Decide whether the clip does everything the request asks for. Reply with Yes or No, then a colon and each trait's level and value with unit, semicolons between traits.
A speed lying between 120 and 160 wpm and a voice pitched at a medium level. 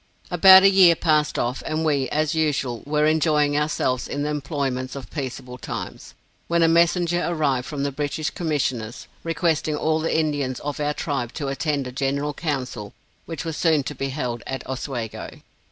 No: average, 175 wpm; medium, 150 Hz